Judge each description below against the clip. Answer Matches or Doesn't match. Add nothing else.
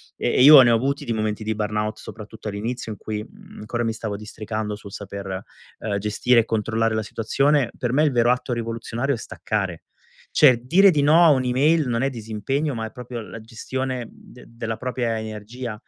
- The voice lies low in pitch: Matches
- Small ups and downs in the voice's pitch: Doesn't match